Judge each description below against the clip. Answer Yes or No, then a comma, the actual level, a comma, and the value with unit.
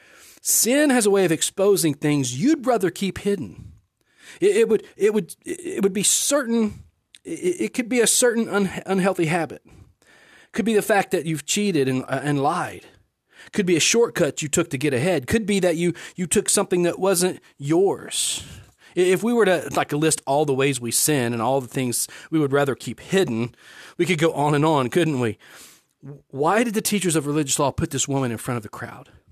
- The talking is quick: Yes, fast, 210 wpm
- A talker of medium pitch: Yes, medium, 175 Hz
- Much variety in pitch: Yes, wide, 6.6 semitones